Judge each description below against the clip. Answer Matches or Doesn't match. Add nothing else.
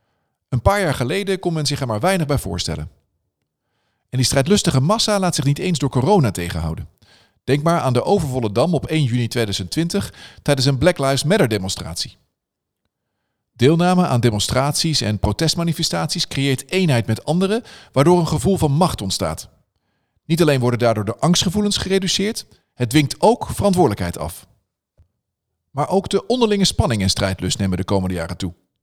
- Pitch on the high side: Doesn't match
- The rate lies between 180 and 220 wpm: Doesn't match